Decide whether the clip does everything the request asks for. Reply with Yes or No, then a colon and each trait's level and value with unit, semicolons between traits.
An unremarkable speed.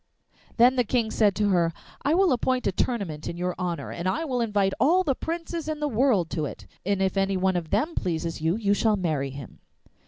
No: fast, 225 wpm